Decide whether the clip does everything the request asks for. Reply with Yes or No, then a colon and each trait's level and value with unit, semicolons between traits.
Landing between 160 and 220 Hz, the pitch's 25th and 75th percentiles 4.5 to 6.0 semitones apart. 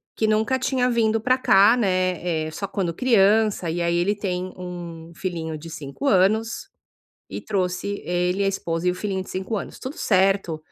No: high, 190 Hz; average, 3.7 semitones